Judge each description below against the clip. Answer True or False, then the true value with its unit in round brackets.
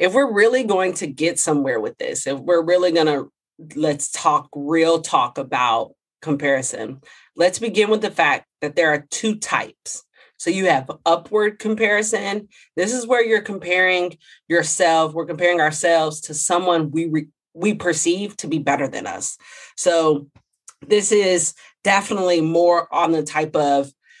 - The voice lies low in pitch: False (170 Hz)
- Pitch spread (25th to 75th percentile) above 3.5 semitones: True (4.5 semitones)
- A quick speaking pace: False (155 wpm)